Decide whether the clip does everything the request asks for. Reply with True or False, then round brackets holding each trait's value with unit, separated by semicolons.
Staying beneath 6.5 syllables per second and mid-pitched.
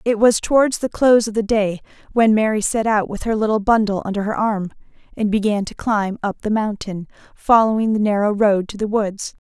False (5.3 syllables/s; 215 Hz)